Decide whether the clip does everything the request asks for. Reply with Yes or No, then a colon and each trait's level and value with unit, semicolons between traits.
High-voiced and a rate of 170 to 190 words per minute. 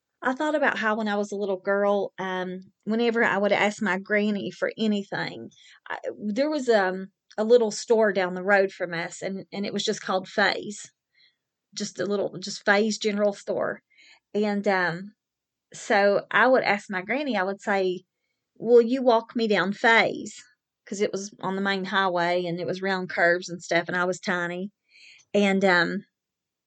Yes: high, 200 Hz; average, 185 wpm